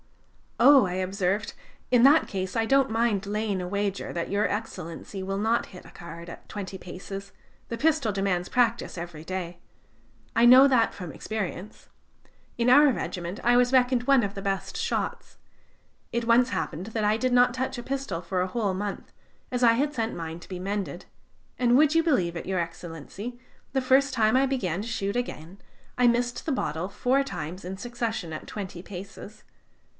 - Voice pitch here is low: No, high, 210 Hz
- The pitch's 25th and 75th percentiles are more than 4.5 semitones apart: Yes, average, 5.0 semitones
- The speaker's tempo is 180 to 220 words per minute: Yes, average, 185 wpm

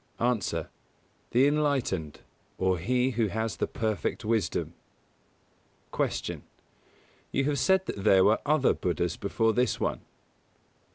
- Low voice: Yes, low, 115 Hz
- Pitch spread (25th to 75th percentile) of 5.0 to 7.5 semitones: Yes, average, 5.3 semitones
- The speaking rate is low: Yes, slow, 130 wpm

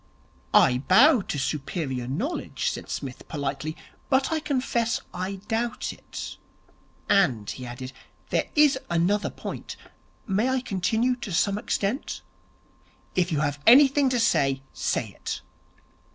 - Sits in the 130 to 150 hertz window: No, high, 195 Hz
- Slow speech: Yes, slow, 130 wpm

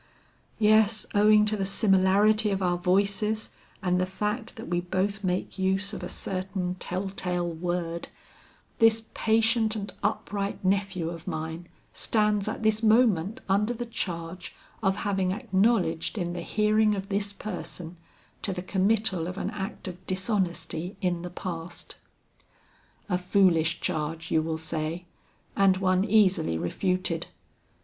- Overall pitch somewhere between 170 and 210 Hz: Yes, high, 190 Hz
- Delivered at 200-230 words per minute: No, average, 140 wpm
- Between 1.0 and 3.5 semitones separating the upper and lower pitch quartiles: Yes, average, 3.1 semitones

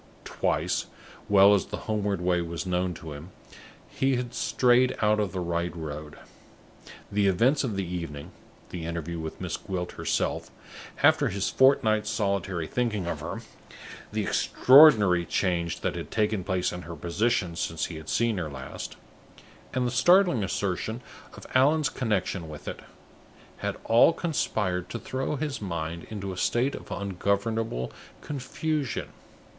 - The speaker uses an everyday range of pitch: No, wide, 5.7 semitones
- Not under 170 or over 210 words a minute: No, average, 150 wpm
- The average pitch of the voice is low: Yes, low, 100 Hz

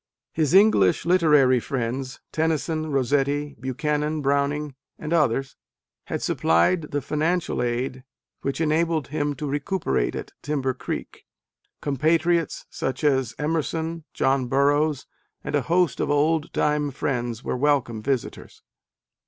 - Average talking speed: No, slow, 120 wpm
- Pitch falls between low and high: Yes, medium, 145 Hz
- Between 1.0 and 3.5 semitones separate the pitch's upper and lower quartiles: Yes, average, 2.9 semitones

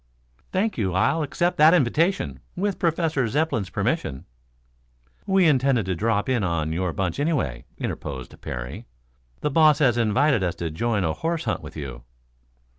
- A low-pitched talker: Yes, low, 120 Hz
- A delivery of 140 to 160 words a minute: Yes, average, 155 wpm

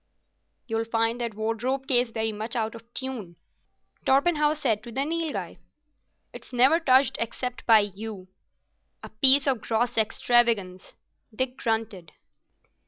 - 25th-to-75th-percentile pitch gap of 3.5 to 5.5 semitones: No, average, 3.1 semitones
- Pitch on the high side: Yes, high, 235 Hz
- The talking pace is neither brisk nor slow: No, slow, 130 wpm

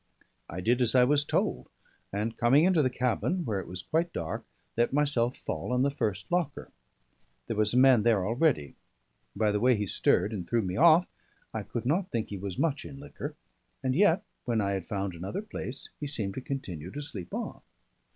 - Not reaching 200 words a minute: No, fast, 205 wpm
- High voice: No, low, 120 Hz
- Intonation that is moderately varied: No, wide, 6.1 semitones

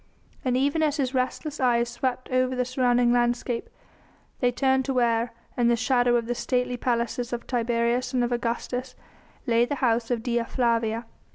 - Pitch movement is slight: Yes, narrow, 1.3 semitones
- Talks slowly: No, average, 175 wpm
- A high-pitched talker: Yes, high, 245 Hz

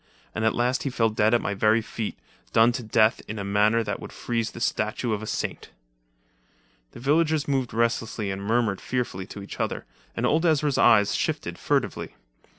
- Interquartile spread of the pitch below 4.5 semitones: Yes, narrow, 2.5 semitones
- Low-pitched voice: Yes, low, 115 Hz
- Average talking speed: Yes, average, 190 wpm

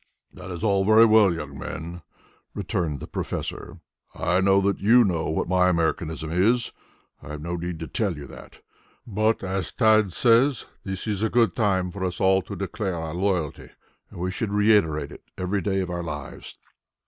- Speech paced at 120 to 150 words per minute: No, average, 185 wpm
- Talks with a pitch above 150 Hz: No, very low, 95 Hz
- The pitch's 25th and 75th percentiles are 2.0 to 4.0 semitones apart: Yes, average, 3.5 semitones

